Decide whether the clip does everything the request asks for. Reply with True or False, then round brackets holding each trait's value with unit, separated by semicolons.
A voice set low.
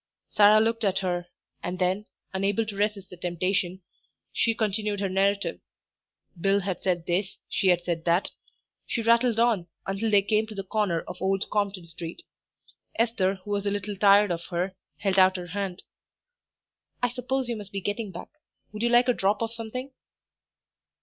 False (200 Hz)